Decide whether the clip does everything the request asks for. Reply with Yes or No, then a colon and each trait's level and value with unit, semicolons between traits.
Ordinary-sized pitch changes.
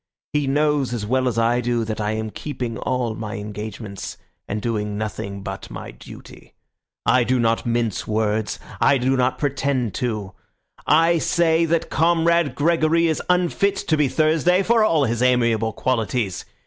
No: wide, 6.0 semitones